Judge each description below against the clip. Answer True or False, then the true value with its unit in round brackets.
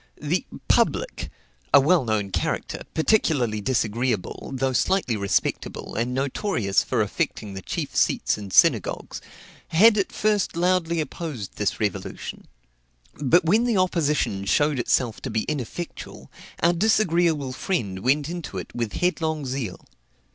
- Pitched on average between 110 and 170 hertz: True (140 Hz)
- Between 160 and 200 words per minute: False (135 wpm)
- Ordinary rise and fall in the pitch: False (7.6 semitones)